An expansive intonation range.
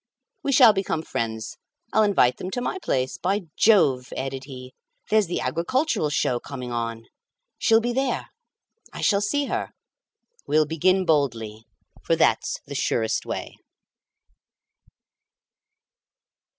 Yes: wide, 8.9 semitones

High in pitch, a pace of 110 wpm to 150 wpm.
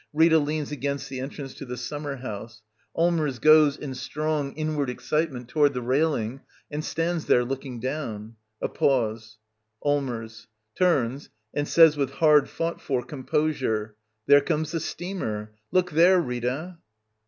No: medium, 140 Hz; average, 145 wpm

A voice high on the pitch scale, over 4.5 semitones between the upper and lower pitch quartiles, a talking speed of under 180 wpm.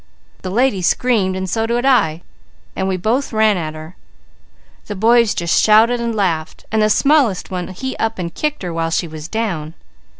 No: high, 205 Hz; average, 5.1 semitones; average, 195 wpm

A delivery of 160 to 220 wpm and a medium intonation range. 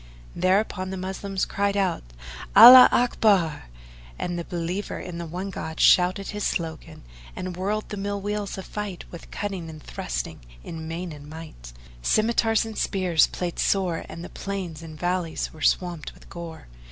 Yes: average, 165 wpm; average, 3.4 semitones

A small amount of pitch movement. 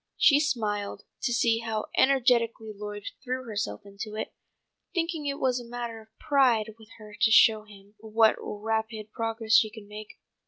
Yes: narrow, 2.3 semitones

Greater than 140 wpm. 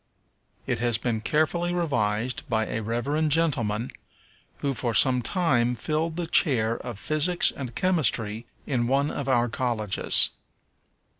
No: slow, 135 wpm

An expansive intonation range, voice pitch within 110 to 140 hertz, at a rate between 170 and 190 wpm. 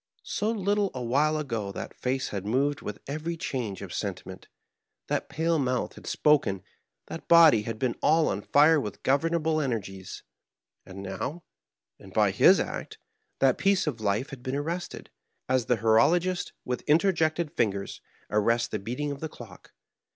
No: wide, 6.1 semitones; low, 135 Hz; average, 160 wpm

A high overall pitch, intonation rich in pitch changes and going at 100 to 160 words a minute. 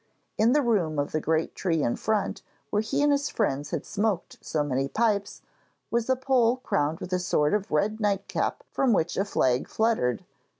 No: high, 200 Hz; wide, 6.6 semitones; average, 195 wpm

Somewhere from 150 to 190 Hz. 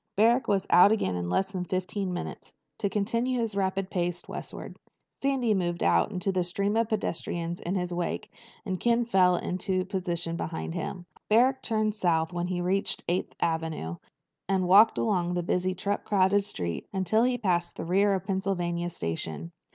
Yes: medium, 185 Hz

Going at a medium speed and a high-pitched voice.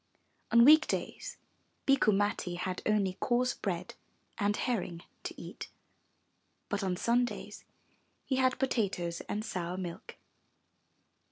No: slow, 115 wpm; high, 205 Hz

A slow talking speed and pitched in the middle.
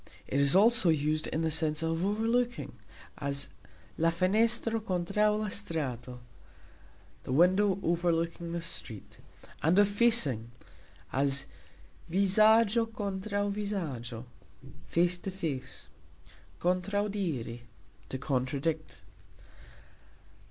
Yes: slow, 95 wpm; medium, 175 Hz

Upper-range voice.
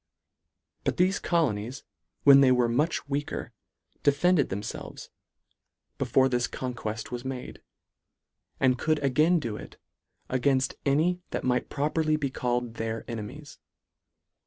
No: low, 135 Hz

